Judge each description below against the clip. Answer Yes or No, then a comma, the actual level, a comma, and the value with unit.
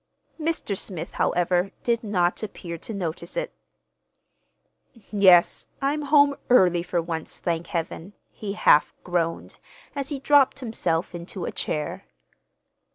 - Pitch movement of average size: No, wide, 7.0 semitones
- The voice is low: No, high, 190 Hz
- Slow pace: Yes, slow, 125 wpm